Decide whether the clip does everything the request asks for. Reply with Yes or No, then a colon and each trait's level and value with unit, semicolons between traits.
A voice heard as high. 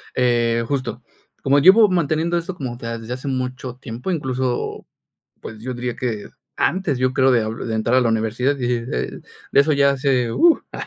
No: low, 130 Hz